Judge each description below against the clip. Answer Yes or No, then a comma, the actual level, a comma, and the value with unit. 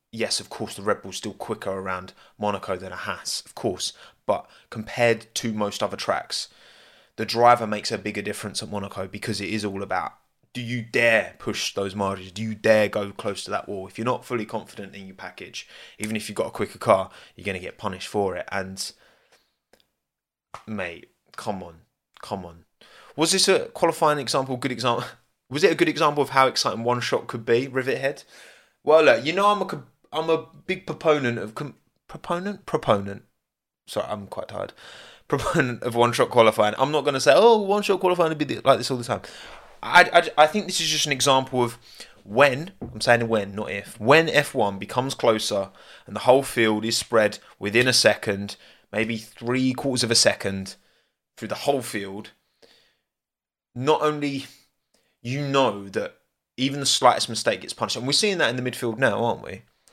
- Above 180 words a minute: Yes, average, 195 wpm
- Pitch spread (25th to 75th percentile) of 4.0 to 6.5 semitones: Yes, average, 5.1 semitones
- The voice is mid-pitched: No, low, 120 Hz